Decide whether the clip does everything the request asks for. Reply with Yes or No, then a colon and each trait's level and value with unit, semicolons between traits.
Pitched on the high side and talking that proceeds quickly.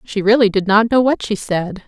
Yes: high, 210 Hz; fast, 255 wpm